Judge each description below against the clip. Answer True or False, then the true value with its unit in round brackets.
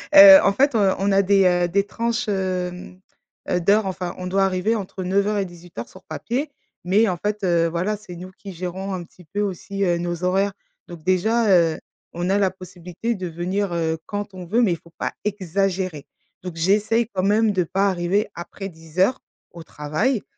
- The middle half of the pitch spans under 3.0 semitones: True (2.6 semitones)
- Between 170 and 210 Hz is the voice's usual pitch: True (190 Hz)